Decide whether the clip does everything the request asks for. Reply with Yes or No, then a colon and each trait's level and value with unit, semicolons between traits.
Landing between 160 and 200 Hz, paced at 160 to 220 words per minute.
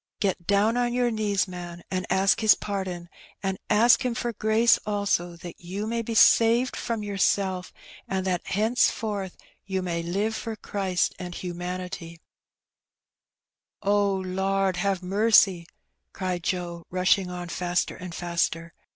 No: high, 190 Hz; average, 150 wpm